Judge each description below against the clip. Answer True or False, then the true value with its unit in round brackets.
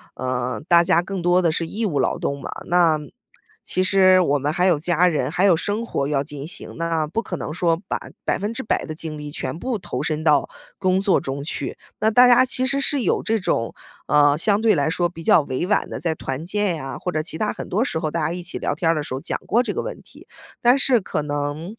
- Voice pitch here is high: False (170 Hz)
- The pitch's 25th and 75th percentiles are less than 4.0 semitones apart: False (4.8 semitones)